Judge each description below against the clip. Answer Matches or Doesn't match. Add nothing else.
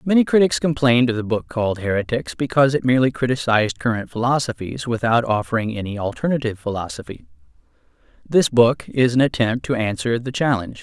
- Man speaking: Matches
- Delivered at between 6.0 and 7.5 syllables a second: Matches